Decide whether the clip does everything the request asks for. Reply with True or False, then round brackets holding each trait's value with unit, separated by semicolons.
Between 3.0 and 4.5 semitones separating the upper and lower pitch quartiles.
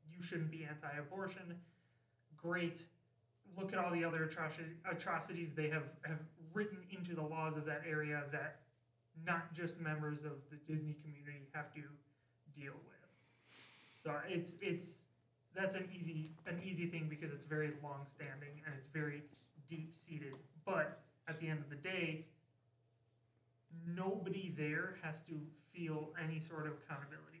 False (2.4 semitones)